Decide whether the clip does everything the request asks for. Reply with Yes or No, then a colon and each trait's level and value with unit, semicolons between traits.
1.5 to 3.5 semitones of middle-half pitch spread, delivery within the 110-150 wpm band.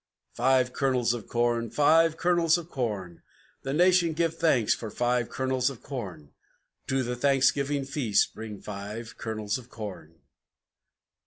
No: average, 4.4 semitones; average, 140 wpm